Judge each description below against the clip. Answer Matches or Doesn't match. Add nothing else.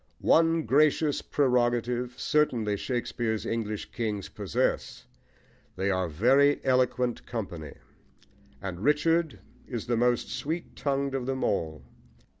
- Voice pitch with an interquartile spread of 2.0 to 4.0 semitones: Doesn't match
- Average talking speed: Doesn't match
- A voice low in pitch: Matches